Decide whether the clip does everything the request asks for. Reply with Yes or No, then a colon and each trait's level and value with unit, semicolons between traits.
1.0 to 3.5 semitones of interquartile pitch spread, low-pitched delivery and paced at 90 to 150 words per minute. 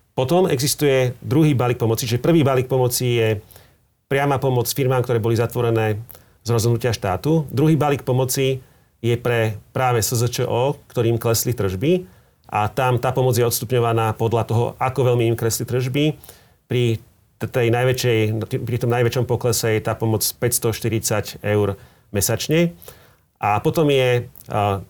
Yes: narrow, 2.4 semitones; low, 120 Hz; average, 145 wpm